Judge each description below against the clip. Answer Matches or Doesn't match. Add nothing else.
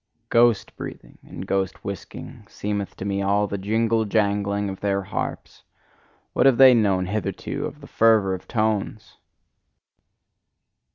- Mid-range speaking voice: Doesn't match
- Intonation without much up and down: Matches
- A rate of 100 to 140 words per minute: Matches